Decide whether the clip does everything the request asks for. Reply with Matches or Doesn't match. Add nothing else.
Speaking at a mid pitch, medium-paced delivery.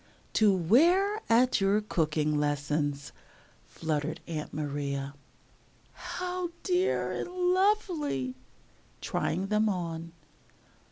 Doesn't match